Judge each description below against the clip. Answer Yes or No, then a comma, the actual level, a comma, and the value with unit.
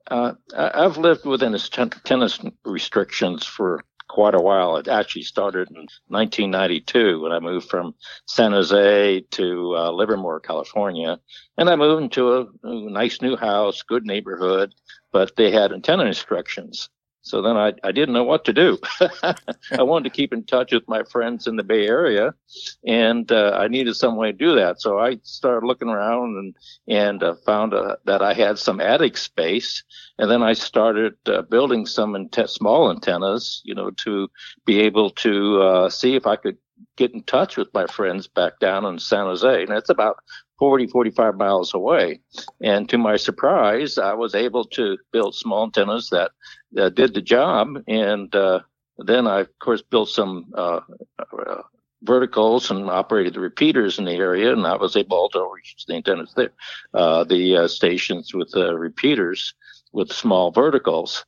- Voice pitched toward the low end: Yes, low, 120 Hz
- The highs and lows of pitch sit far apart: Yes, wide, 7.5 semitones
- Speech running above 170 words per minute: Yes, average, 180 wpm